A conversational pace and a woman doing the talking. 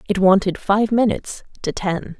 Yes: average, 165 wpm; female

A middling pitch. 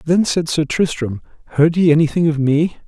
Yes: medium, 155 Hz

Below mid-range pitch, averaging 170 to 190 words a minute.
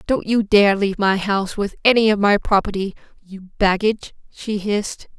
No: high, 205 Hz; average, 175 wpm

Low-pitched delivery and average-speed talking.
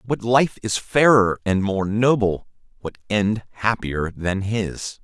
Yes: low, 105 Hz; average, 145 wpm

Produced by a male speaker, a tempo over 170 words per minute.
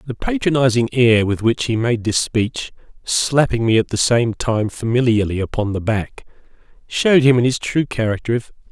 Yes: male; average, 185 wpm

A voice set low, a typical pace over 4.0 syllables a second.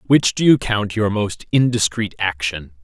Yes: low, 105 Hz; 4.4 syllables/s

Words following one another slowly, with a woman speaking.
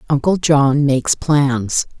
Yes: slow, 120 wpm; female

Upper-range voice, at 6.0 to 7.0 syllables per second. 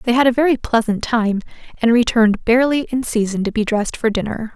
Yes: high, 230 Hz; 6.1 syllables/s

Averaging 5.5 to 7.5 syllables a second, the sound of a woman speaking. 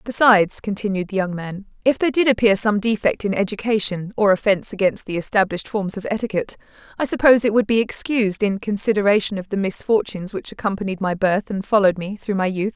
Yes: 6.4 syllables/s; female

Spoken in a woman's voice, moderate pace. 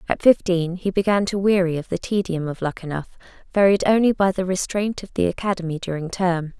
Yes: female; average, 190 wpm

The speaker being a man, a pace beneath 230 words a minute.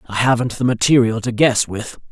Yes: male; average, 200 wpm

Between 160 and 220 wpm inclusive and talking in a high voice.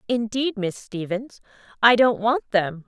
No: average, 145 wpm; high, 215 Hz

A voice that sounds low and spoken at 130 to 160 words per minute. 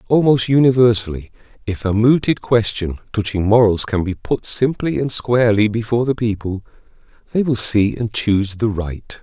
Yes: low, 110 Hz; average, 155 wpm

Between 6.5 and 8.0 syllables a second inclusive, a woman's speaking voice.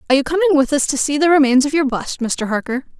Yes: 6.9 syllables/s; female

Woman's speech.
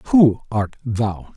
No: male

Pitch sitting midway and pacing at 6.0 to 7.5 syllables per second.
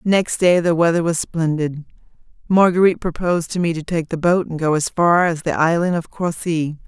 No: medium, 170 Hz; 5.3 syllables/s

